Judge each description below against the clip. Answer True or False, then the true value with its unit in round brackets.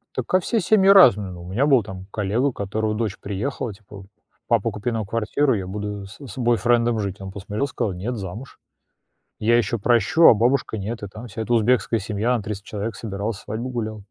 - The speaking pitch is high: False (110 Hz)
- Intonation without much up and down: False (3.1 semitones)